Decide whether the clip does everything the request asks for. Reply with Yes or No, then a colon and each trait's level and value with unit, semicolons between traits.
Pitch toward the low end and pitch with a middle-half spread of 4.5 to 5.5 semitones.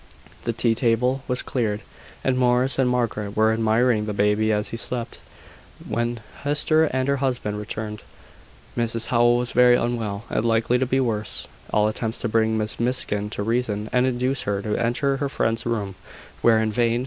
No: low, 115 Hz; narrow, 2.4 semitones